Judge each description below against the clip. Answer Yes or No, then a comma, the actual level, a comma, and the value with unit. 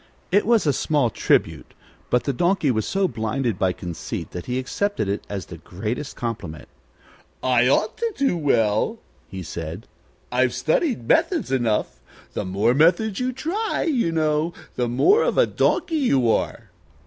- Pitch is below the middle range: Yes, low, 130 Hz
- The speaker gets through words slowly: No, average, 160 wpm